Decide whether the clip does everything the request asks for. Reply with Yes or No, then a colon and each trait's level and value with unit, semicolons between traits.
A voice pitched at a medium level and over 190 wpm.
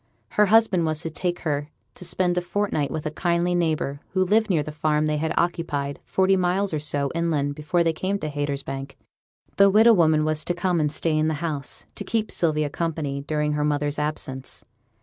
Yes: medium, 155 Hz; fast, 205 wpm